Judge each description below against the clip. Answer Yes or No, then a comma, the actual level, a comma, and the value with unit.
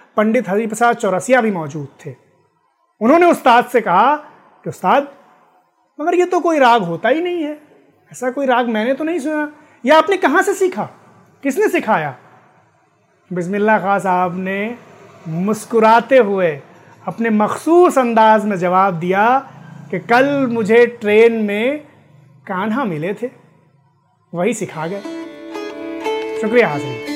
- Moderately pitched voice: No, high, 230 Hz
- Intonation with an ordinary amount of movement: No, wide, 7.2 semitones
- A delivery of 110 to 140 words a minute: Yes, average, 135 wpm